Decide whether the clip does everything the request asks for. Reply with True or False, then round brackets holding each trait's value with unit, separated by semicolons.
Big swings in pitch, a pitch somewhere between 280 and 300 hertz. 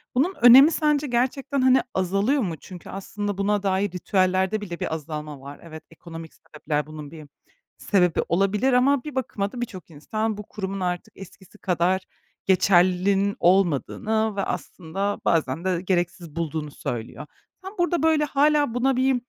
False (6.2 semitones; 195 Hz)